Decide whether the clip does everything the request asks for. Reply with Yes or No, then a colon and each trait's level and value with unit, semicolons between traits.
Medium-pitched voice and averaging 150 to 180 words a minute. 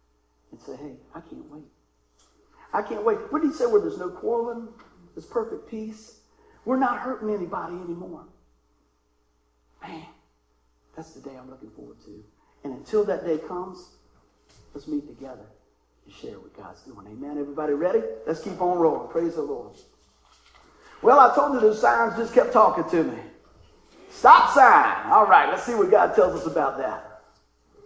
Yes: medium, 180 Hz; average, 170 wpm